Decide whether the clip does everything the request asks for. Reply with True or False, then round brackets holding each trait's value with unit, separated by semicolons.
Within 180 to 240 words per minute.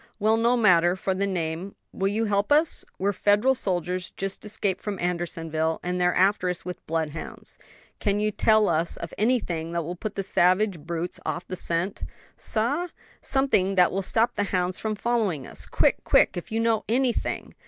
True (185 wpm)